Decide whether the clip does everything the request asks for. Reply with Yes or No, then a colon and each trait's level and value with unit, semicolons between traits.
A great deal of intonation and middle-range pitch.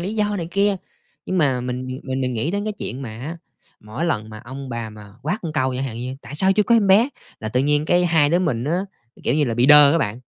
Yes: wide, 6.1 semitones; medium, 145 Hz